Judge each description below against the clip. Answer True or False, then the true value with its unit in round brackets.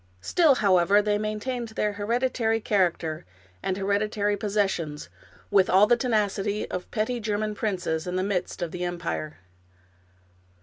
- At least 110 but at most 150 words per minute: True (140 wpm)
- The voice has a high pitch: True (205 Hz)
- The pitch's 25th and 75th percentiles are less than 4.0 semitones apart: True (2.8 semitones)